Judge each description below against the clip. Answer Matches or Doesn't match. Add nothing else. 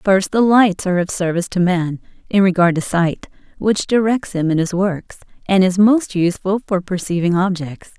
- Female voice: Matches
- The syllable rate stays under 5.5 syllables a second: Matches